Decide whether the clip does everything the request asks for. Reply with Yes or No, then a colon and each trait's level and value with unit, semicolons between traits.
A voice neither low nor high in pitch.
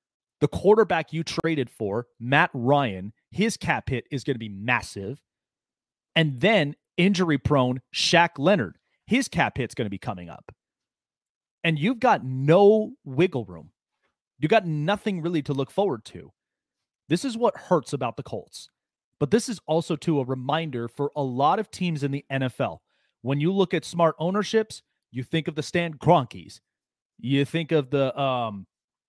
Yes: medium, 150 Hz